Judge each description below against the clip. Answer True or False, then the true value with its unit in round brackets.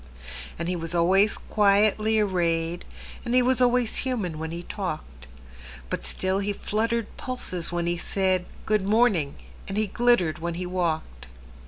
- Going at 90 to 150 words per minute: True (140 wpm)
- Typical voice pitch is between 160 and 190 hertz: True (185 Hz)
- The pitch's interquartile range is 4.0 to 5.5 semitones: True (4.4 semitones)